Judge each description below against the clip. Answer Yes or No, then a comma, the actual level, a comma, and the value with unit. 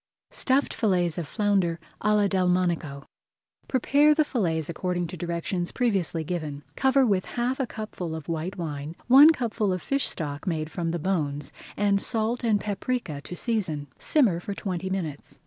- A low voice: No, medium, 185 Hz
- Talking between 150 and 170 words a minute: Yes, average, 165 wpm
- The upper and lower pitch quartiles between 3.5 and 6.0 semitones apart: Yes, average, 5.1 semitones